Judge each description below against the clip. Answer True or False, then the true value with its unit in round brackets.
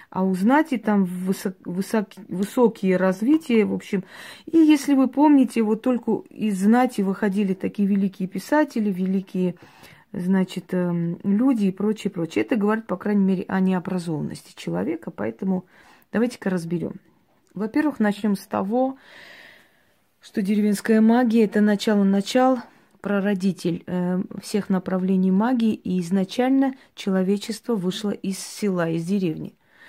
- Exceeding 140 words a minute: False (120 wpm)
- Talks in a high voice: True (200 Hz)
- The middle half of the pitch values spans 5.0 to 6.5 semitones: False (3.2 semitones)